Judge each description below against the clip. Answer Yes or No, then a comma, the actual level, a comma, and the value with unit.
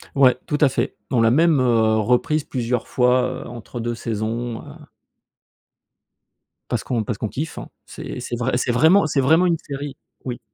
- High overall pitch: No, low, 125 Hz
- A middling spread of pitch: Yes, average, 3.2 semitones